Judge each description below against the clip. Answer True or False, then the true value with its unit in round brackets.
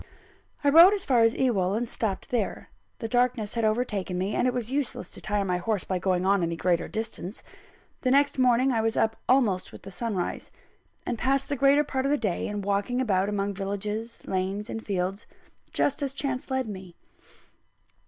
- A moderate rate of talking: True (195 wpm)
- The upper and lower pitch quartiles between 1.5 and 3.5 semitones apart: False (4.6 semitones)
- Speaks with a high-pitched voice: True (220 Hz)